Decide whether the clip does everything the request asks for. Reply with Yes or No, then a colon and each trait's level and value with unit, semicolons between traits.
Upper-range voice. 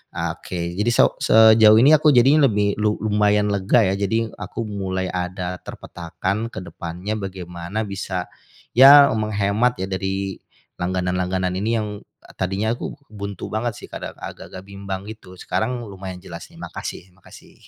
No: low, 100 Hz